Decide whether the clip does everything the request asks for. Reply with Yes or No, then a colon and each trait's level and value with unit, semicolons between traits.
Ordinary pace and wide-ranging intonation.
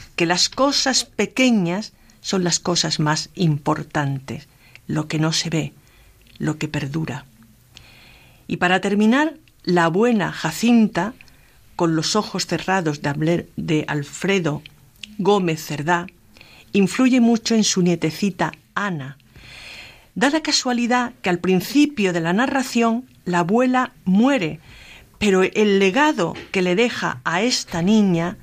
No: slow, 120 wpm; wide, 5.9 semitones